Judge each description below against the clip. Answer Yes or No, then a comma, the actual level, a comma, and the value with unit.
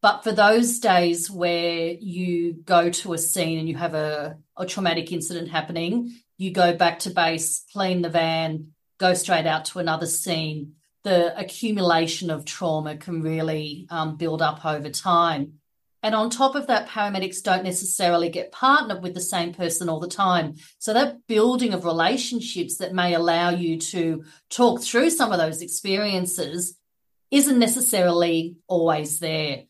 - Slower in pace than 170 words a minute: Yes, average, 160 wpm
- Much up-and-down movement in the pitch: No, average, 2.9 semitones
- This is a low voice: No, medium, 175 Hz